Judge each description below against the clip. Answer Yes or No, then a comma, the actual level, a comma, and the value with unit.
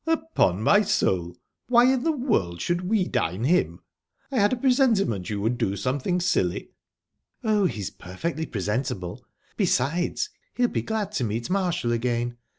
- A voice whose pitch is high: No, medium, 165 Hz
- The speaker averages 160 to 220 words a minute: No, average, 150 wpm